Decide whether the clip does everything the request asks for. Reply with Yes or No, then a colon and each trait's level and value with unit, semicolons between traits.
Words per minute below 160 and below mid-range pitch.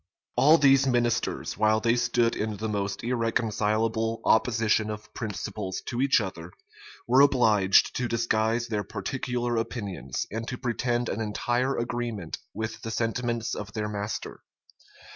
Yes: average, 140 wpm; low, 115 Hz